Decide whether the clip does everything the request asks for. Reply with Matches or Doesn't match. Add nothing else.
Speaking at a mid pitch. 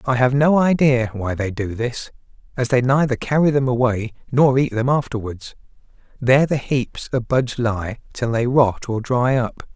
Doesn't match